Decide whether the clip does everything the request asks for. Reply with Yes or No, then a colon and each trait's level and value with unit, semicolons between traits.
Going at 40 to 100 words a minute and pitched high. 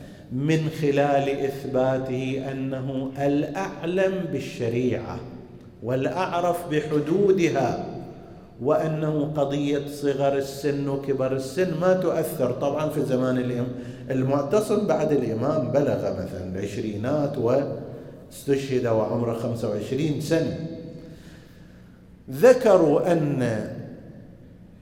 No: average, 75 wpm; medium, 140 Hz